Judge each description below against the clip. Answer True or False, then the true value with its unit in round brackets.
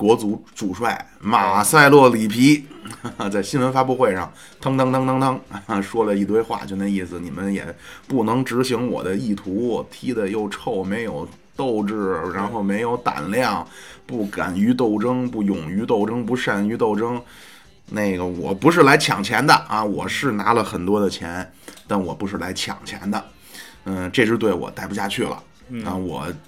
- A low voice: True (105 Hz)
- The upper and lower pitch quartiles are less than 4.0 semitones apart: False (4.3 semitones)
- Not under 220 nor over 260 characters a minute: True (245 characters per minute)